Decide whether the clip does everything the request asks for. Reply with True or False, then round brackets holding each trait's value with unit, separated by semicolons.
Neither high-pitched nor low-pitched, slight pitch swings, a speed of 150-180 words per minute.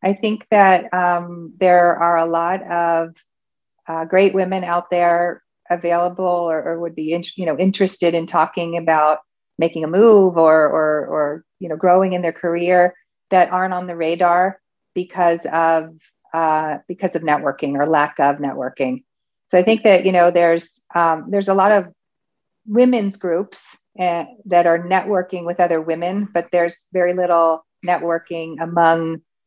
True (175 Hz; 2.1 semitones; 165 wpm)